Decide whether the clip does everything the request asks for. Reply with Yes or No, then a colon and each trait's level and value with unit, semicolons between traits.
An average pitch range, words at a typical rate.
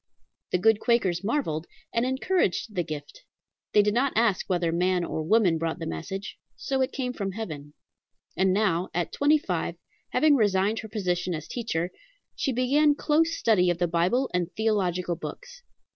No: wide, 6.0 semitones; average, 170 wpm